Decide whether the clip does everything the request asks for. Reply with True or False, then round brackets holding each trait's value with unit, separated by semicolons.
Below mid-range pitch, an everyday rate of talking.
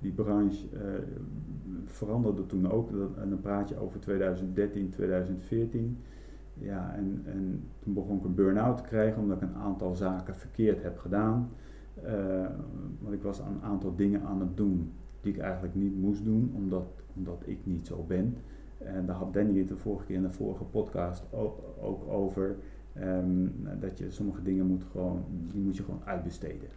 True (95 Hz; 180 wpm)